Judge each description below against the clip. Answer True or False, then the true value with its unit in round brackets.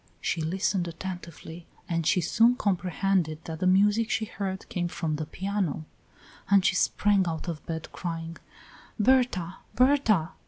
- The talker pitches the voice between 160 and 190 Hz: True (185 Hz)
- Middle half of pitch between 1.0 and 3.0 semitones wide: False (3.5 semitones)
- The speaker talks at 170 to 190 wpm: False (145 wpm)